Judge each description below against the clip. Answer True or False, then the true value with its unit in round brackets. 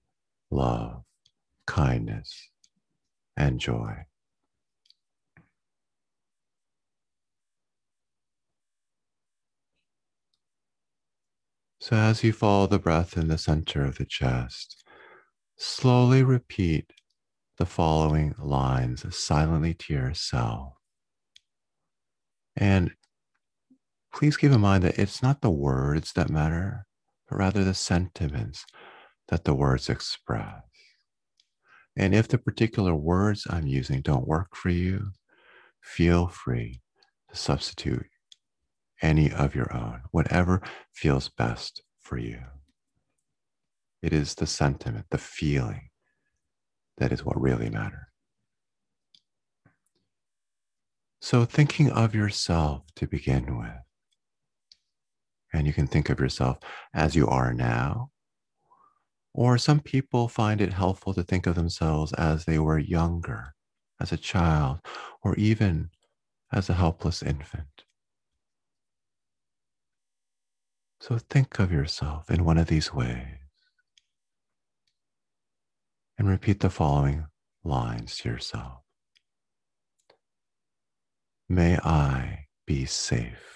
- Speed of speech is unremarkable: False (100 wpm)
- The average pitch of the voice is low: True (85 Hz)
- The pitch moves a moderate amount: False (5.9 semitones)